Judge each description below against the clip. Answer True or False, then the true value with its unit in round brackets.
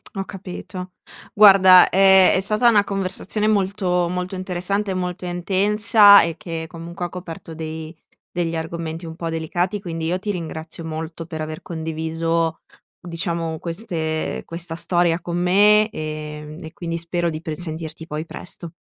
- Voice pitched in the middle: True (175 Hz)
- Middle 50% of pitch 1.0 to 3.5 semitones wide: True (2.6 semitones)